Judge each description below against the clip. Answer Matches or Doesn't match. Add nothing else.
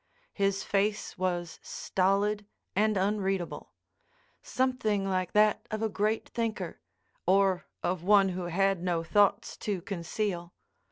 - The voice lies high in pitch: Matches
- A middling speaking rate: Doesn't match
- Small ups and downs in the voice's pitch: Matches